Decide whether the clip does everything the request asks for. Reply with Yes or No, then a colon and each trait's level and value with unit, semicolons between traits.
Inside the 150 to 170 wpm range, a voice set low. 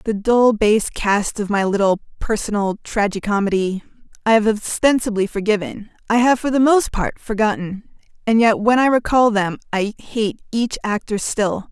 No: average, 155 wpm; high, 215 Hz